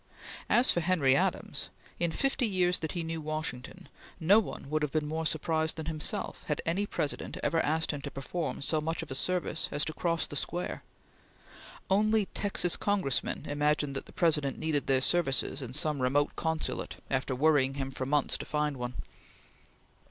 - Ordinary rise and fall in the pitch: Yes, average, 3.2 semitones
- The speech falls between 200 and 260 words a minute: No, average, 180 wpm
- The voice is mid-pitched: Yes, medium, 155 Hz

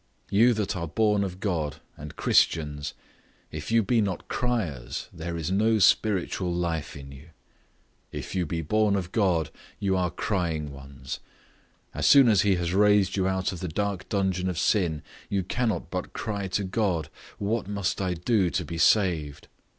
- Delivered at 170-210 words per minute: Yes, average, 175 wpm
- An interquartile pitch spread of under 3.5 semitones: No, average, 3.8 semitones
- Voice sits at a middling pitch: No, very low, 95 Hz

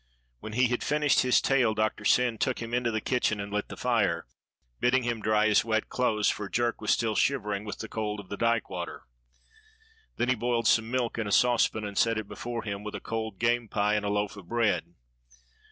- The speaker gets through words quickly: Yes, fast, 220 wpm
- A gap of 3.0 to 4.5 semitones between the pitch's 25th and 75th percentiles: No, narrow, 2.4 semitones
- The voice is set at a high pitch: No, low, 110 Hz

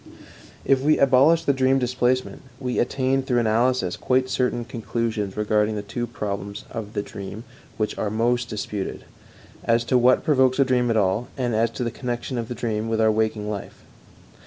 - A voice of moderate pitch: No, low, 120 Hz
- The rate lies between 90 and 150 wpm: No, average, 180 wpm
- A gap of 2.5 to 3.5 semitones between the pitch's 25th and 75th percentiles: Yes, average, 2.9 semitones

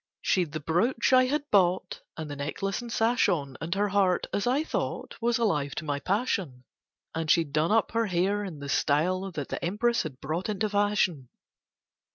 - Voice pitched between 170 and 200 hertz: Yes, medium, 185 Hz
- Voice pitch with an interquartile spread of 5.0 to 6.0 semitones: Yes, wide, 5.6 semitones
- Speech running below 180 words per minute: No, average, 195 wpm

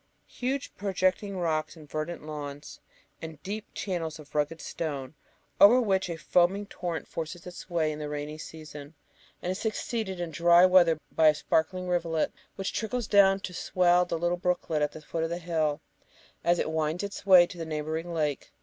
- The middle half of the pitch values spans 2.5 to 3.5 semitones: Yes, average, 3.0 semitones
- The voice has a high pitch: No, medium, 170 Hz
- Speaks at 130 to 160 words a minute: No, average, 185 wpm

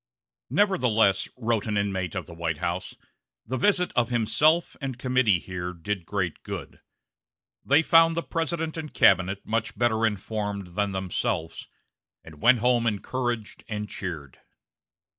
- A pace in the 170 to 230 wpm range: No, average, 140 wpm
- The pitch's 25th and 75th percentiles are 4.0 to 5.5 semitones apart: Yes, average, 5.2 semitones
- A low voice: Yes, low, 110 Hz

